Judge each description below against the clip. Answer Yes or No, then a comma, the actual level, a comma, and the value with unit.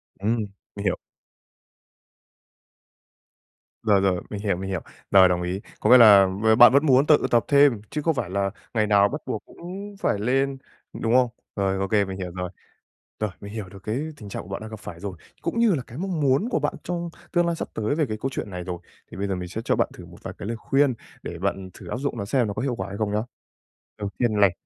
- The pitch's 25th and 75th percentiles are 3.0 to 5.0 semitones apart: No, wide, 5.6 semitones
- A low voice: Yes, low, 110 Hz